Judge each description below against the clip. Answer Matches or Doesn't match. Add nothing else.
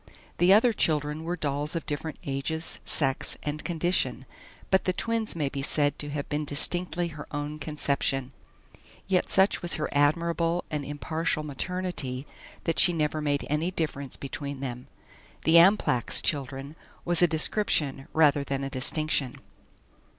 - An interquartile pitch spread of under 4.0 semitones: Matches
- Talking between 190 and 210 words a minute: Doesn't match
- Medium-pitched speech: Matches